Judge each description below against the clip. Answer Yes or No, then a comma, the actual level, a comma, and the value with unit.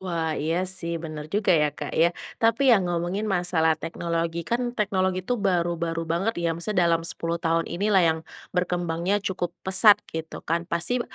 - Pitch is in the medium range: Yes, medium, 175 Hz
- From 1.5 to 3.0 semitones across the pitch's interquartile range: Yes, narrow, 2.4 semitones